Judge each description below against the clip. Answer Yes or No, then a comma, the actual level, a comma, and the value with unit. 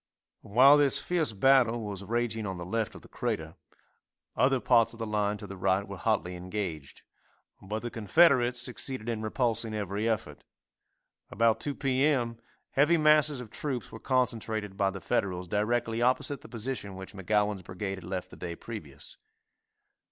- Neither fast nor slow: Yes, average, 165 wpm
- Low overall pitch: Yes, low, 110 Hz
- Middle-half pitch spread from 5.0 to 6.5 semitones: No, average, 4.2 semitones